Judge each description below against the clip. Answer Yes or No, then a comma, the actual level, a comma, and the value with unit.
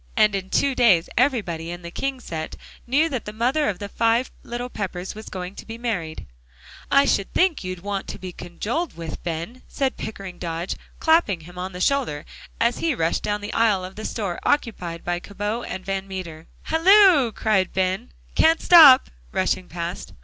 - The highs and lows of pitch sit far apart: Yes, wide, 5.7 semitones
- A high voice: Yes, high, 205 Hz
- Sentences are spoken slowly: No, average, 185 wpm